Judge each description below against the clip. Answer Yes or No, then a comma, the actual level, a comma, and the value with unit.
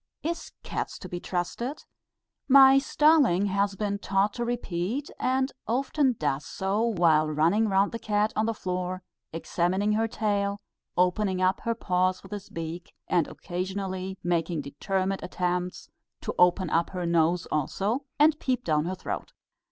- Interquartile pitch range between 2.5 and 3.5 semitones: No, average, 3.9 semitones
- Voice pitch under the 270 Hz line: Yes, high, 190 Hz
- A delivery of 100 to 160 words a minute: Yes, average, 150 wpm